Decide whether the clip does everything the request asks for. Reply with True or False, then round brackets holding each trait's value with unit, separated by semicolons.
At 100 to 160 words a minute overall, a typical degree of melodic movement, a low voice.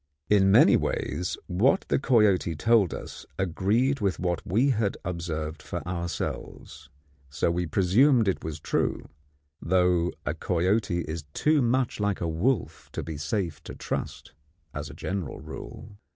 True (150 wpm; 4.5 semitones; 95 Hz)